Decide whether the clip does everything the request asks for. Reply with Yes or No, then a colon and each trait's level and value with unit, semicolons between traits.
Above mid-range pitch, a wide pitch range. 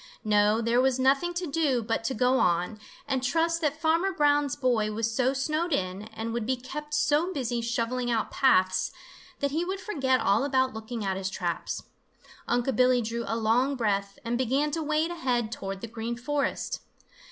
No: very high, 250 Hz; average, 4.5 semitones